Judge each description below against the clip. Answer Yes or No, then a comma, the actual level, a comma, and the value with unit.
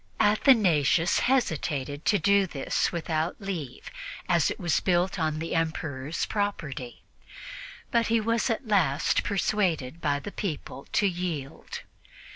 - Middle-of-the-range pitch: Yes, medium, 170 Hz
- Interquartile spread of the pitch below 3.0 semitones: No, average, 5.3 semitones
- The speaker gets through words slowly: Yes, slow, 125 wpm